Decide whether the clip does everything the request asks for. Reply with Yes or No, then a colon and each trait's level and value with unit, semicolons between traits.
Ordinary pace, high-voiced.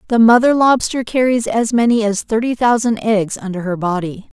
Yes: average, 175 wpm; high, 225 Hz